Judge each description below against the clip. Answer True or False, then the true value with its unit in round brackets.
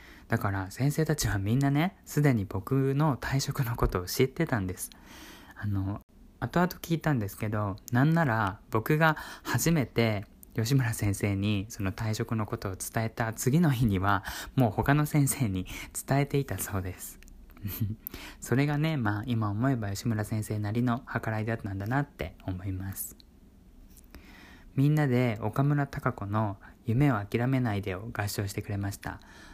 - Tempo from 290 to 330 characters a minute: True (295 characters per minute)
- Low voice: True (115 Hz)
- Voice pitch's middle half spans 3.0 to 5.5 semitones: True (5.2 semitones)